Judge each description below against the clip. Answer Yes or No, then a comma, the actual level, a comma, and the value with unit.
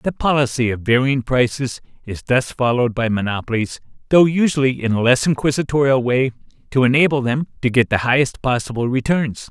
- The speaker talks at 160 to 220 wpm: Yes, average, 165 wpm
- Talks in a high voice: No, low, 130 Hz